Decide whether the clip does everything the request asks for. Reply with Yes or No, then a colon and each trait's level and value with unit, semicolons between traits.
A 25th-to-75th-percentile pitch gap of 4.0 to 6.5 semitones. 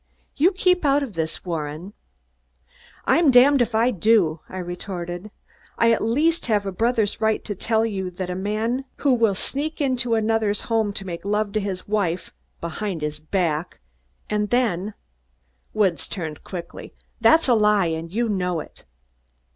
Yes: average, 4.6 semitones